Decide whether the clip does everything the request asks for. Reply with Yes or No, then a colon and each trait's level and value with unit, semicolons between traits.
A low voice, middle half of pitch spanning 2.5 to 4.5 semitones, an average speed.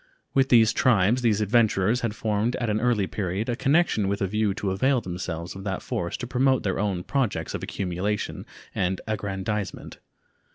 Yes: low, 105 Hz; average, 3.9 semitones; average, 175 wpm